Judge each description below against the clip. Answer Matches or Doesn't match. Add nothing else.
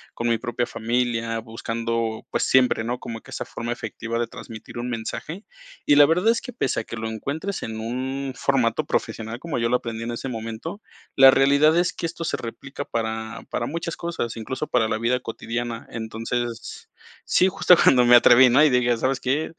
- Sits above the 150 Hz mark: Doesn't match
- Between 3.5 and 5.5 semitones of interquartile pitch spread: Doesn't match